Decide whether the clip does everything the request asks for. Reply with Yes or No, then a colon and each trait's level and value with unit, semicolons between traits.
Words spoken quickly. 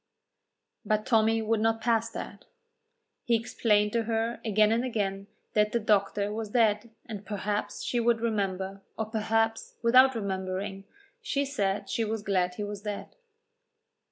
No: average, 150 wpm